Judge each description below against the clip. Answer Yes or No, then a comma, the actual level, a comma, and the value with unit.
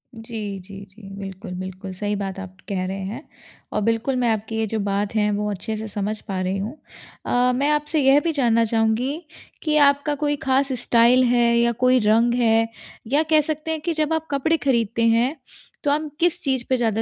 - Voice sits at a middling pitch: No, high, 230 Hz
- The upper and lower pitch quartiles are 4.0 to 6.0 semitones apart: Yes, average, 5.0 semitones